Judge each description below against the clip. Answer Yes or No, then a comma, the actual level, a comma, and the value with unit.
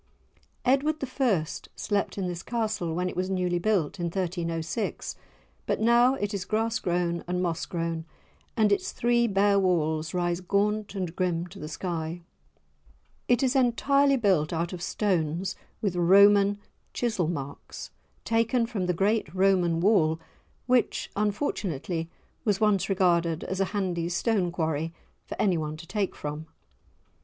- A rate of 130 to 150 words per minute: Yes, average, 145 wpm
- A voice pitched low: No, medium, 185 Hz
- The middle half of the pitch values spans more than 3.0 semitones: Yes, average, 3.9 semitones